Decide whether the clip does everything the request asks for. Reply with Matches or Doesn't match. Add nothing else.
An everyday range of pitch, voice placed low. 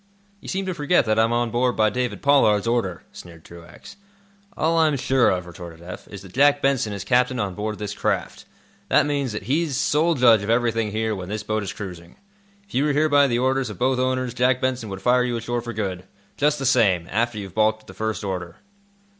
Matches